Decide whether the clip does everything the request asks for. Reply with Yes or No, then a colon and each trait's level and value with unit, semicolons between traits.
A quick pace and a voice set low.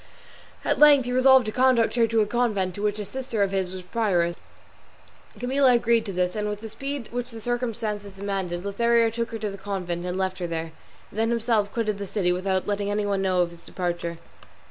No: fast, 215 wpm; high, 210 Hz